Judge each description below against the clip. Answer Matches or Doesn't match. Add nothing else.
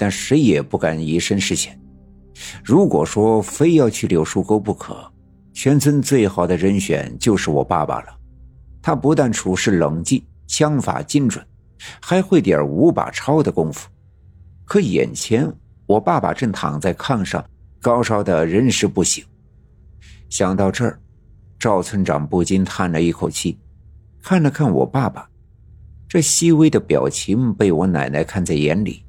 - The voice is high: Doesn't match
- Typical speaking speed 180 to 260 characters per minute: Matches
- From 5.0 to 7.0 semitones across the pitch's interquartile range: Matches